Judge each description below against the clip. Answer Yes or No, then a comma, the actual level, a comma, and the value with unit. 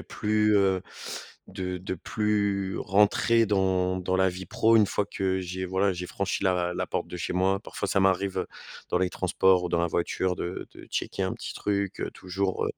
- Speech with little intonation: Yes, narrow, 1.4 semitones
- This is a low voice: Yes, very low, 95 Hz